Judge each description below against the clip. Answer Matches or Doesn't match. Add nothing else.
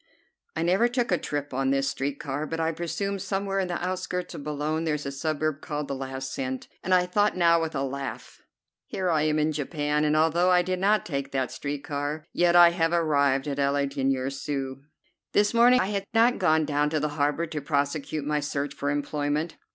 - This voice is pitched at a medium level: Matches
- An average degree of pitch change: Matches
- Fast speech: Matches